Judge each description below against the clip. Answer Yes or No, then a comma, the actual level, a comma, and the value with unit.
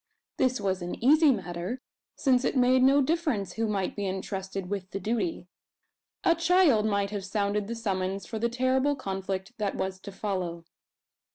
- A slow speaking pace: No, average, 170 wpm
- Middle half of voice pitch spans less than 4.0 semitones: No, average, 5.1 semitones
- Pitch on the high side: Yes, high, 205 Hz